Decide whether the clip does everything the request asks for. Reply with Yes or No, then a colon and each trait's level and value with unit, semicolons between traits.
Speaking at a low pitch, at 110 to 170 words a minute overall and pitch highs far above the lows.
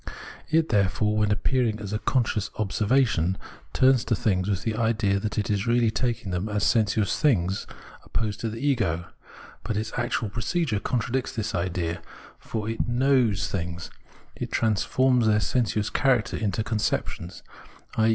No: low, 110 Hz; average, 150 wpm; average, 3.0 semitones